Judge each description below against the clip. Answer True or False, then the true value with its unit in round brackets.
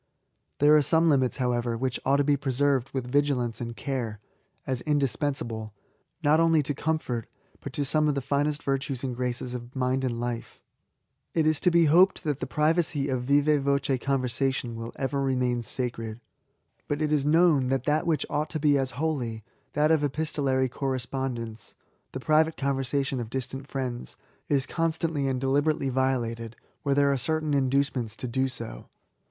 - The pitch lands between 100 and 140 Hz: True (135 Hz)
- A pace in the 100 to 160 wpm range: False (180 wpm)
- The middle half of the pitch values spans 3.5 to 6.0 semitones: False (2.9 semitones)